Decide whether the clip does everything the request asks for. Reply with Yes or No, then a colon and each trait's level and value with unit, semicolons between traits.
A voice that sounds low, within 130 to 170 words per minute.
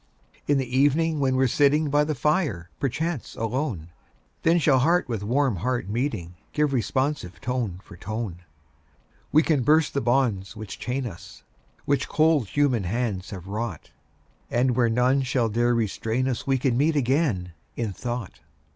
Yes: low, 125 Hz; average, 160 wpm